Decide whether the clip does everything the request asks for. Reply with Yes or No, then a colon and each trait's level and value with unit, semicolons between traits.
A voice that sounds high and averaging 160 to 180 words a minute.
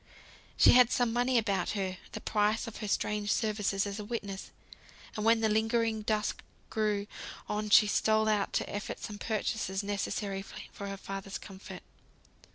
Yes: high, 210 Hz; average, 165 wpm